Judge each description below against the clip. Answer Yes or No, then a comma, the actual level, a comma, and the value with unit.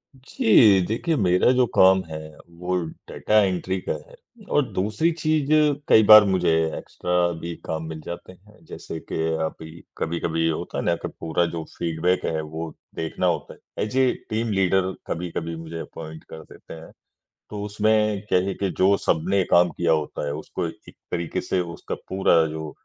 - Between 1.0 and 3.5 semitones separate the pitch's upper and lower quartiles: No, average, 4.1 semitones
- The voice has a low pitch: Yes, very low, 90 Hz